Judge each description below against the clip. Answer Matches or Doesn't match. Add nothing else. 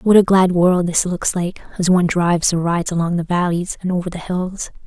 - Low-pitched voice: Doesn't match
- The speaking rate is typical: Doesn't match